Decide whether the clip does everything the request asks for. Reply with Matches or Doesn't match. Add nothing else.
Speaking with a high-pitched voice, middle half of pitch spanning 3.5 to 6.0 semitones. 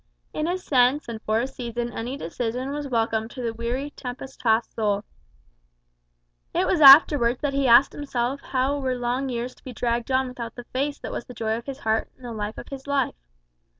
Doesn't match